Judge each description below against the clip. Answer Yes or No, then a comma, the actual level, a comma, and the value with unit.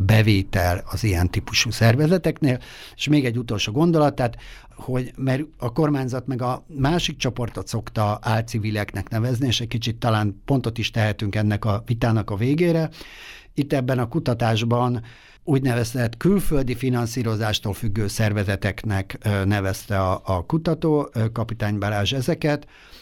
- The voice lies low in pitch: Yes, low, 120 Hz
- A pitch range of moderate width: Yes, average, 4.4 semitones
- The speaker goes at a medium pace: Yes, average, 135 wpm